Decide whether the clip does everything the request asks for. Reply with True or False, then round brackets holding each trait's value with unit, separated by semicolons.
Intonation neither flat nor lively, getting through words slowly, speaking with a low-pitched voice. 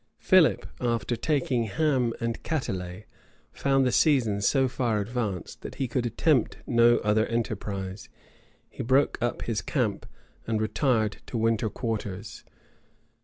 True (3.3 semitones; 130 wpm; 115 Hz)